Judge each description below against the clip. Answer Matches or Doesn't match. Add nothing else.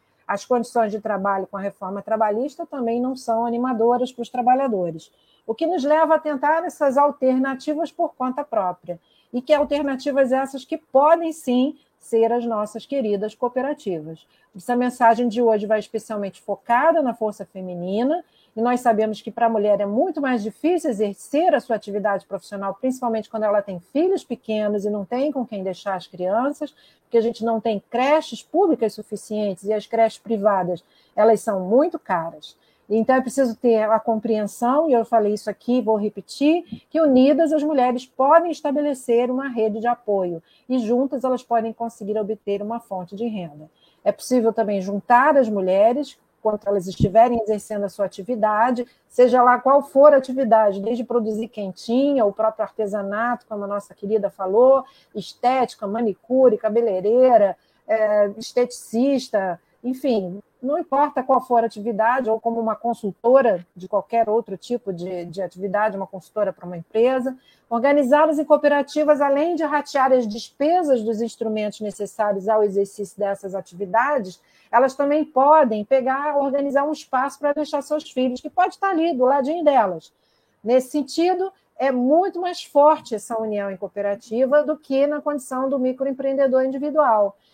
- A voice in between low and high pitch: Doesn't match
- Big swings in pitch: Doesn't match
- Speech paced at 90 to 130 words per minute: Doesn't match